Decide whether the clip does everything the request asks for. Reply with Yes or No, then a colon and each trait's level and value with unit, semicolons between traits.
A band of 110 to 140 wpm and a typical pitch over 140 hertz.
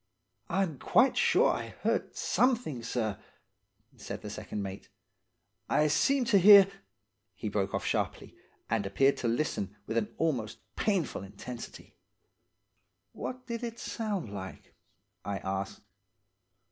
No: slow, 135 wpm; low, 120 Hz